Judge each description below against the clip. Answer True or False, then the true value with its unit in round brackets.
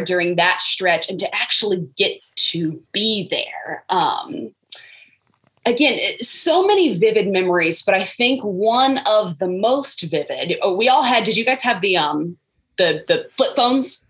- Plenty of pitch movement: True (6.3 semitones)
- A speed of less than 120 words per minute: False (160 wpm)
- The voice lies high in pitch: True (215 Hz)